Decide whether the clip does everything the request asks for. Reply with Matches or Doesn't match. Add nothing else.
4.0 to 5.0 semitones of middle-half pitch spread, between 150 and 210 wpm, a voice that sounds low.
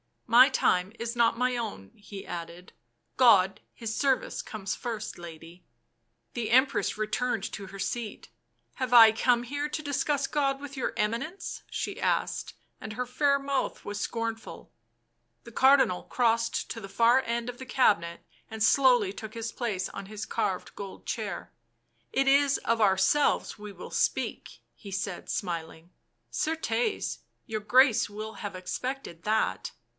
Doesn't match